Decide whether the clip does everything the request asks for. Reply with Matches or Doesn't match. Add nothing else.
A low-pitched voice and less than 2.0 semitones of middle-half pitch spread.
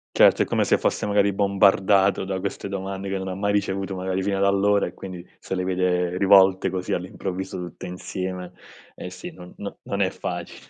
Matches